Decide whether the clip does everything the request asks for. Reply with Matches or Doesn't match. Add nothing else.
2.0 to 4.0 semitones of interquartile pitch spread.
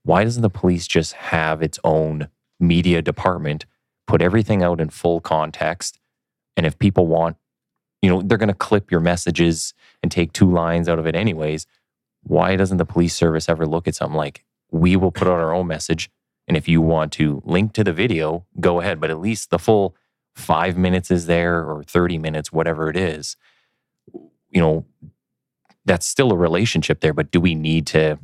Matches